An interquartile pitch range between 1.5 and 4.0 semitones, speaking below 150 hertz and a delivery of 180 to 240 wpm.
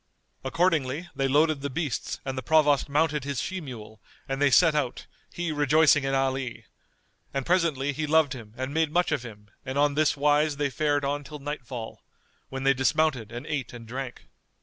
Yes: narrow, 2.6 semitones; medium, 140 Hz; average, 190 wpm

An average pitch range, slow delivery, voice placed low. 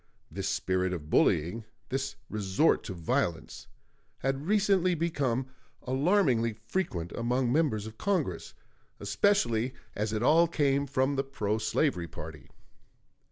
No: wide, 6.7 semitones; slow, 120 wpm; low, 125 Hz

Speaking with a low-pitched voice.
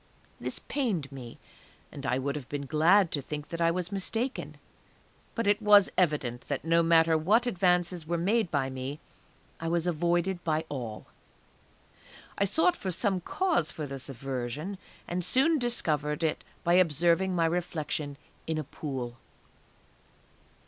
No: medium, 165 Hz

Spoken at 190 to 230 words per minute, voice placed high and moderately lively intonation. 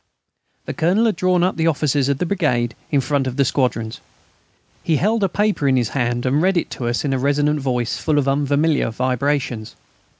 No: fast, 205 wpm; medium, 140 Hz; average, 4.3 semitones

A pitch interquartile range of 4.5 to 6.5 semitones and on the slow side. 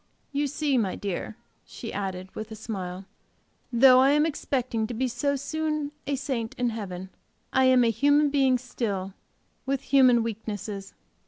No: average, 4.8 semitones; average, 160 wpm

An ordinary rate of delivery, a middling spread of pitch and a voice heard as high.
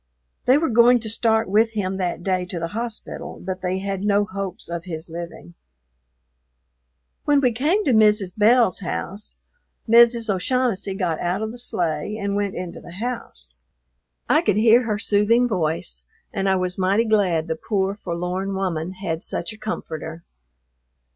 Yes: average, 165 wpm; average, 3.9 semitones; high, 195 Hz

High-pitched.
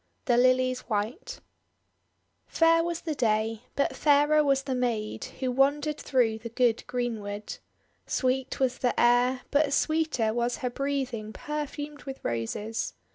Yes: very high, 255 Hz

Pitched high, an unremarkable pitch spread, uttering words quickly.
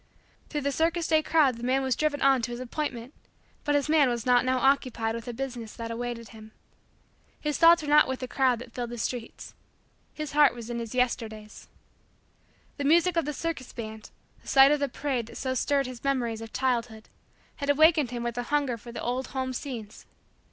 Yes: very high, 255 Hz; average, 3.4 semitones; fast, 210 wpm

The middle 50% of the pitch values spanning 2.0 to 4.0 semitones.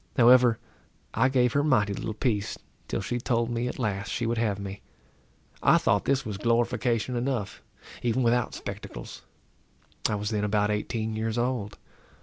Yes: average, 2.8 semitones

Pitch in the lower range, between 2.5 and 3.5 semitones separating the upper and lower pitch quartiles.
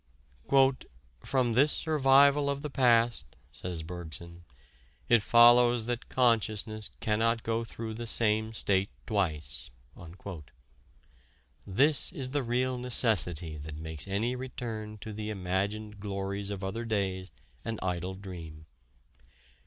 No: low, 110 Hz; average, 4.2 semitones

